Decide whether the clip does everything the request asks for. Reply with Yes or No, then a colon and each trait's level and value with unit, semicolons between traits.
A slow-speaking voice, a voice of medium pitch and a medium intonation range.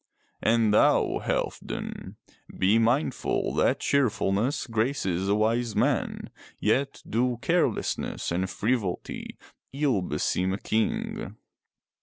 No: slow, 100 wpm; low, 115 Hz; average, 4.6 semitones